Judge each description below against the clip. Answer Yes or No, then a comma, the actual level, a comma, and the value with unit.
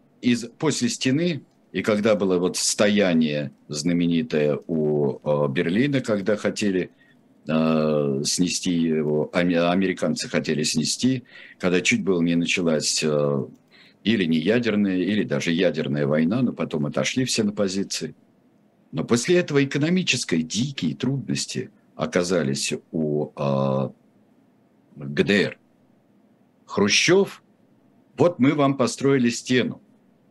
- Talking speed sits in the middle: No, slow, 105 wpm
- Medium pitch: No, very low, 90 Hz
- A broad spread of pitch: Yes, wide, 8.2 semitones